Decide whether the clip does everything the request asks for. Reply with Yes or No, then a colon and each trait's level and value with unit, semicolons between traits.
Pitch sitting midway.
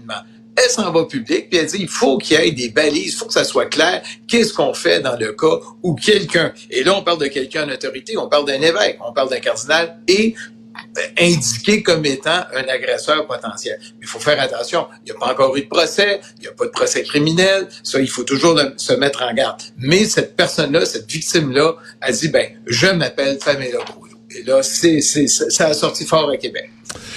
Yes: medium, 160 Hz